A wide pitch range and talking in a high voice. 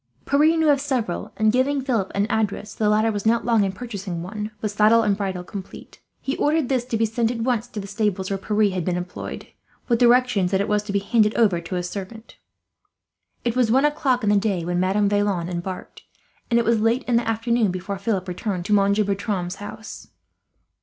No: average, 3.2 semitones; high, 210 Hz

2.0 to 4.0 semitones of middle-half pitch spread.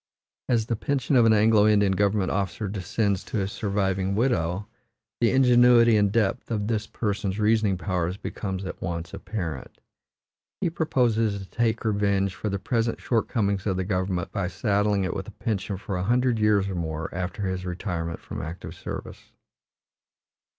Yes: average, 3.0 semitones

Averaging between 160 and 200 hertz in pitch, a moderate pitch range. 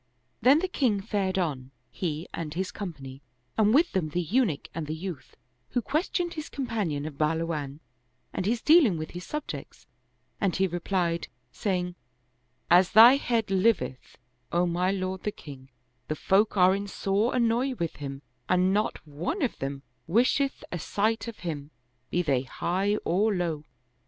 No: medium, 185 Hz; wide, 5.9 semitones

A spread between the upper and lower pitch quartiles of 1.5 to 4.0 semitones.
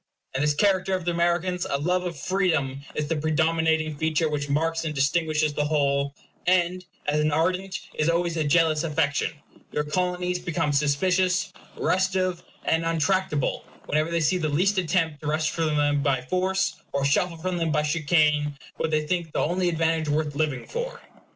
Yes: average, 3.1 semitones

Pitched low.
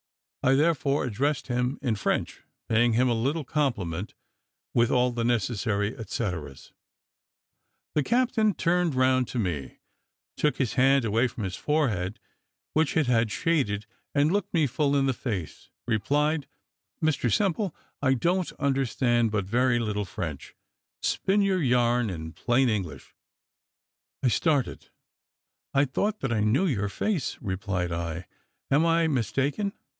Yes: low, 125 Hz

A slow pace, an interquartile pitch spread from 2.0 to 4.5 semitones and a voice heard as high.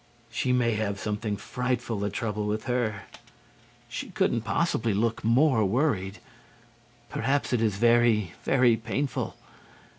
No: slow, 125 wpm; average, 2.8 semitones; low, 115 Hz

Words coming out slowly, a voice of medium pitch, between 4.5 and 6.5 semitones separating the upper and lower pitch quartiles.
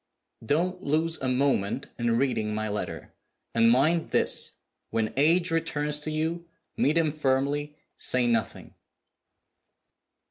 Yes: slow, 120 wpm; medium, 145 Hz; average, 5.3 semitones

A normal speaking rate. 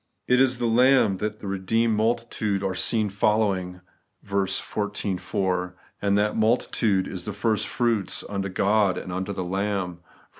Yes: average, 155 wpm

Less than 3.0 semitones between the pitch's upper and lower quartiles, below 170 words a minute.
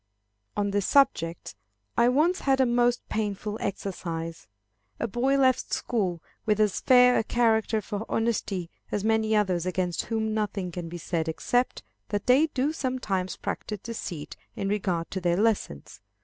No: average, 4.7 semitones; average, 155 wpm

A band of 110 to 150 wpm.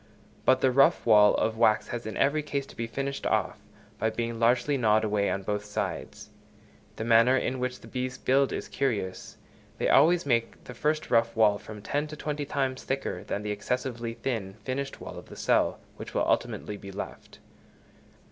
No: average, 190 wpm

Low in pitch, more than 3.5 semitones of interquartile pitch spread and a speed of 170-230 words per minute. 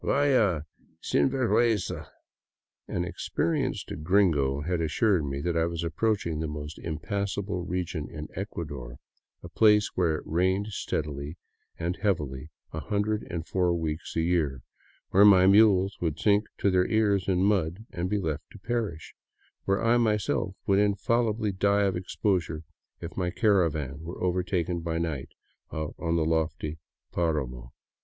No: very low, 90 Hz; average, 4.2 semitones; average, 145 wpm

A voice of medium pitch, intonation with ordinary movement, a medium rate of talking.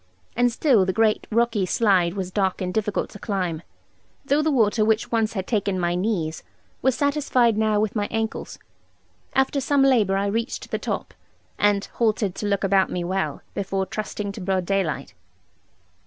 No: high, 205 Hz; average, 3.1 semitones; average, 170 wpm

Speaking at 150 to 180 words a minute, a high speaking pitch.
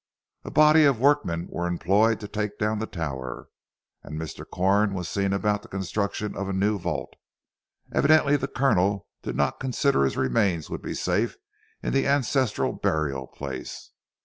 No: average, 170 wpm; low, 100 Hz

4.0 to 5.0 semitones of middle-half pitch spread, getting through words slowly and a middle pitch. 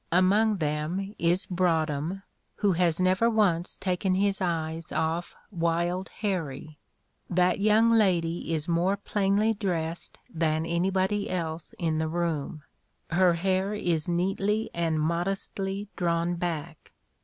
No: average, 2.9 semitones; slow, 120 wpm; medium, 175 Hz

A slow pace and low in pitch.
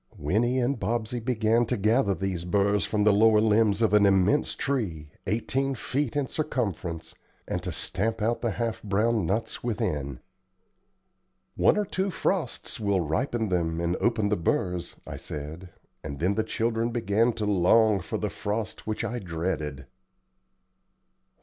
No: average, 155 wpm; low, 105 Hz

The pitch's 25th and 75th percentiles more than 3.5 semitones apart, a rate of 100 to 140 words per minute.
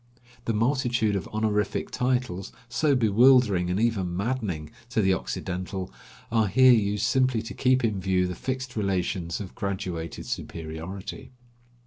Yes: average, 4.9 semitones; slow, 135 wpm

